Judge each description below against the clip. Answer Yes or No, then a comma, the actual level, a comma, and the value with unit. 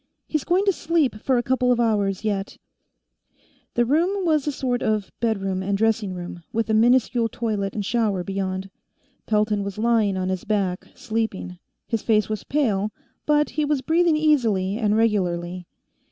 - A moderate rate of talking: Yes, average, 170 wpm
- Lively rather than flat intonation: No, average, 4.6 semitones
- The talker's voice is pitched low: No, high, 220 Hz